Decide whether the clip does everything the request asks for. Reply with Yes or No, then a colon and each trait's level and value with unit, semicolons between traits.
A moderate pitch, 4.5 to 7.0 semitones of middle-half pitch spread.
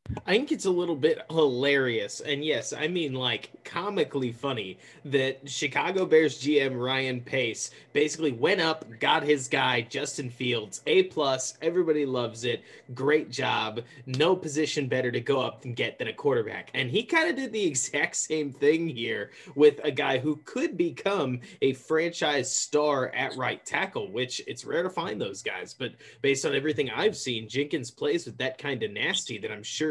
No: medium, 150 Hz; average, 3.3 semitones